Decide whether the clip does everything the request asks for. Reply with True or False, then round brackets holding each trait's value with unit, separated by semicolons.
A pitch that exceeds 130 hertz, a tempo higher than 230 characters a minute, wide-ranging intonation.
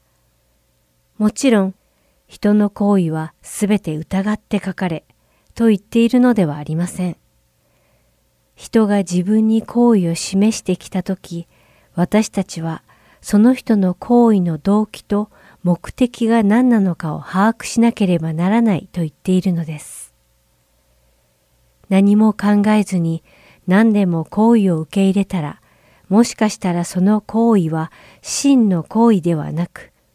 False (190 Hz; 250 characters per minute; 4.8 semitones)